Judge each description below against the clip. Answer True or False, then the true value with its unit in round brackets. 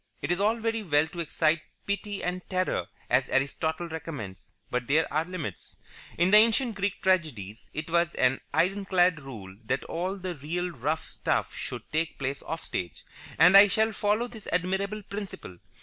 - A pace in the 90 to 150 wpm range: False (170 wpm)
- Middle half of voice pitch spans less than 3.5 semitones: False (5.2 semitones)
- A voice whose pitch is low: False (175 Hz)